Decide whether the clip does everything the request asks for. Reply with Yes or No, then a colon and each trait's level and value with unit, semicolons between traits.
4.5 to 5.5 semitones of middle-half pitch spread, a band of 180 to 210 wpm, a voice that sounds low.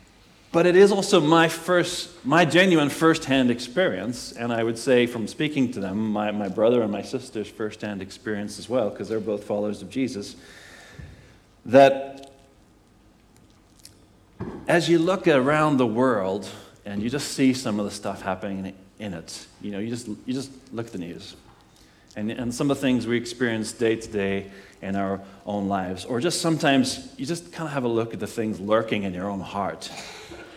Yes: average, 5.1 semitones; average, 185 wpm; low, 115 Hz